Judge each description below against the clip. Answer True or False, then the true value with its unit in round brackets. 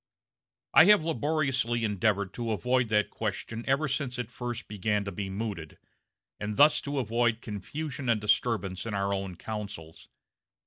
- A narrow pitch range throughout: False (3.9 semitones)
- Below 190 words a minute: True (150 wpm)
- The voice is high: False (115 Hz)